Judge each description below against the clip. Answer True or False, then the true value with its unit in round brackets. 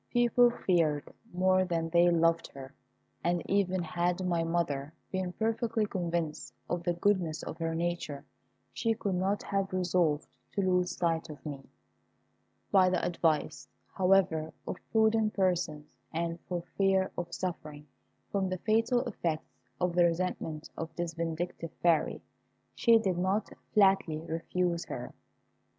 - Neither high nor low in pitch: True (175 Hz)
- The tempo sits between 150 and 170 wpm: False (140 wpm)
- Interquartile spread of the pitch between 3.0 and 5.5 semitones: False (2.5 semitones)